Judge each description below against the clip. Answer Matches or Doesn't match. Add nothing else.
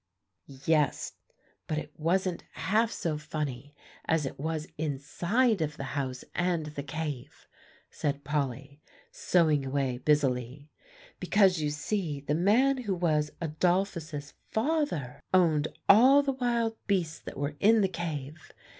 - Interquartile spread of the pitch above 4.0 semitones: Matches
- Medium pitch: Matches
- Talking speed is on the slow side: Matches